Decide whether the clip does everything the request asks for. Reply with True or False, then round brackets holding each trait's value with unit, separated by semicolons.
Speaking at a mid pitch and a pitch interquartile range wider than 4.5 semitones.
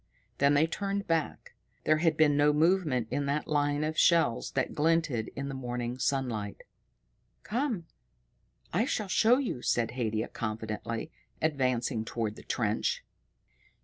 True (145 Hz; 5.2 semitones)